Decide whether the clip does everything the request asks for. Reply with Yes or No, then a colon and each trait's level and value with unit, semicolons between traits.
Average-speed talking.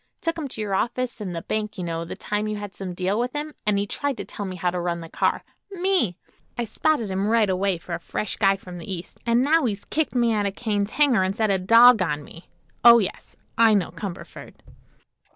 No: fast, 240 wpm